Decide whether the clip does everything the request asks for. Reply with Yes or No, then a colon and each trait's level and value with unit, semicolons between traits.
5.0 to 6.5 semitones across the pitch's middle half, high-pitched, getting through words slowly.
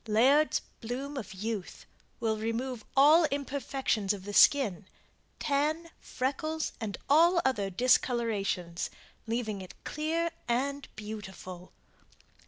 Yes: average, 5.3 semitones; high, 245 Hz; slow, 105 wpm